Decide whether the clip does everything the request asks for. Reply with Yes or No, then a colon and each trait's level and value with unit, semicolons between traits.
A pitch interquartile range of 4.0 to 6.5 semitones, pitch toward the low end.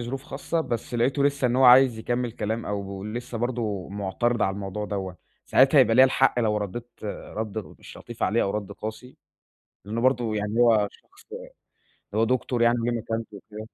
No: average, 2.8 semitones; low, 115 Hz